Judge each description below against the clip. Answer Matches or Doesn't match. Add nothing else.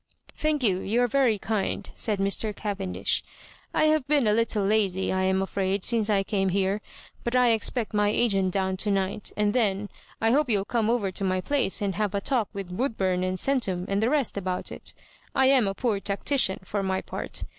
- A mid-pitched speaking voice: Doesn't match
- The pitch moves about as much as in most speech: Matches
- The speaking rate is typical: Doesn't match